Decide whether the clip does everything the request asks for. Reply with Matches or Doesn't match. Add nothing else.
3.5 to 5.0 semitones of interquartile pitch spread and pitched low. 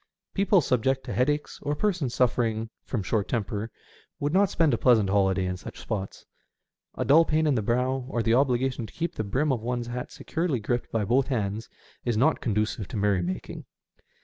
Matches